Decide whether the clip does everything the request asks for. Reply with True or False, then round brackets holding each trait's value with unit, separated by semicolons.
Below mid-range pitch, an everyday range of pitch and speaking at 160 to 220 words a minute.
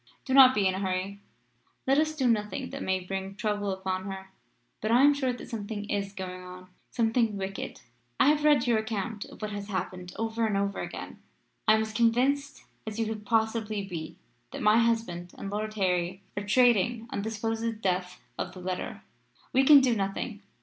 False (210 Hz; 3.2 semitones; 200 wpm)